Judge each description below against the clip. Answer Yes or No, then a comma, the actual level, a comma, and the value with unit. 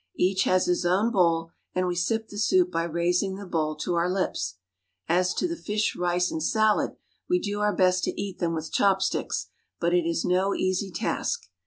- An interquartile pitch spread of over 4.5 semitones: No, average, 2.9 semitones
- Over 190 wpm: Yes, average, 200 wpm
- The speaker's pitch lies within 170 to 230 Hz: Yes, medium, 185 Hz